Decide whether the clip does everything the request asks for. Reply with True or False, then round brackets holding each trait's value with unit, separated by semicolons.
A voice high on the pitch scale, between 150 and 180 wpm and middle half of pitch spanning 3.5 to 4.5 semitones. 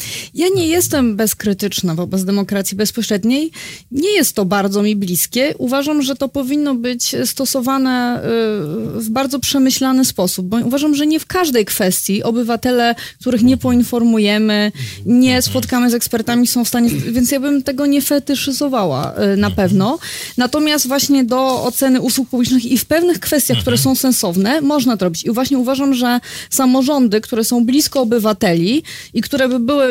True (250 Hz; 155 wpm; 4.1 semitones)